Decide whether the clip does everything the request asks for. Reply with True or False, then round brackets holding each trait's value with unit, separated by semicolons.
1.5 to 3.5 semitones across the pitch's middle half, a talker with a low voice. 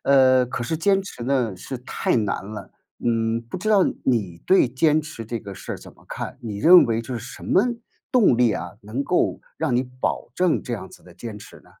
False (4.1 semitones; 120 Hz)